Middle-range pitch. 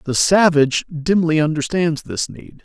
Yes: medium, 160 Hz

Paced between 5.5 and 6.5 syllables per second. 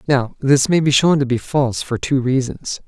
No: 4.9 syllables/s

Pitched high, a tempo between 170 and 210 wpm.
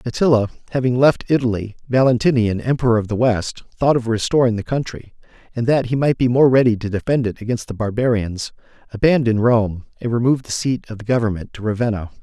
No: low, 115 Hz; average, 180 wpm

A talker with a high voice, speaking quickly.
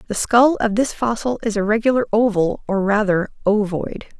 No: high, 215 Hz; average, 170 wpm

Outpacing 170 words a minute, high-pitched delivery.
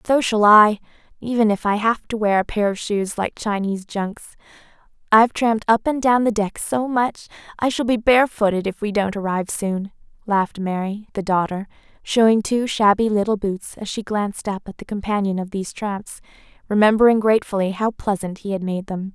Yes: average, 190 wpm; high, 210 Hz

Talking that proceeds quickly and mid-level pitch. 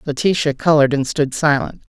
No: average, 155 wpm; medium, 150 Hz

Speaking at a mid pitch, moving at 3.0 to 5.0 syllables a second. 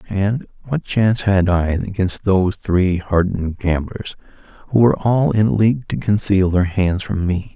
No: very low, 95 Hz; 4.6 syllables/s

